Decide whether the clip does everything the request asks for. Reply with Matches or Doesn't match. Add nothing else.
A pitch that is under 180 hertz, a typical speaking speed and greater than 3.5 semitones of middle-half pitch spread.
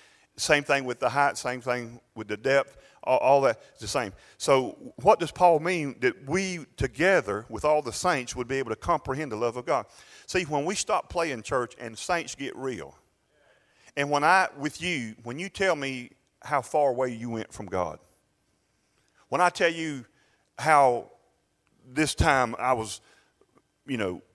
Matches